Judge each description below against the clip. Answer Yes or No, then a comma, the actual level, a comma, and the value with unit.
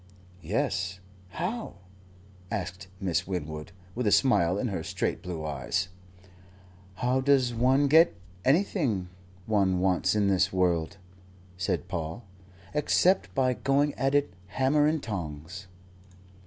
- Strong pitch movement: Yes, wide, 6.9 semitones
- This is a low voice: Yes, low, 100 Hz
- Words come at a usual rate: No, slow, 120 wpm